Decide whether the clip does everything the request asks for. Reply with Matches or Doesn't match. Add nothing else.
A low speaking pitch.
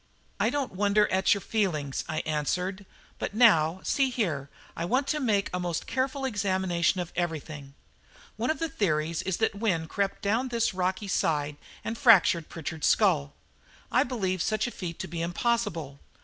Doesn't match